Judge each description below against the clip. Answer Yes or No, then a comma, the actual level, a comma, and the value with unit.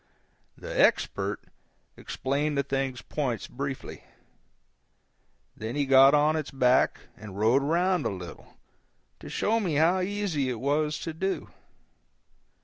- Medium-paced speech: No, slow, 130 wpm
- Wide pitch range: No, average, 3.8 semitones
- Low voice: No, medium, 145 Hz